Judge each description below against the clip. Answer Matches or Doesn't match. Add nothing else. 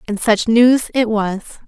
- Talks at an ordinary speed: Matches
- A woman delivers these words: Matches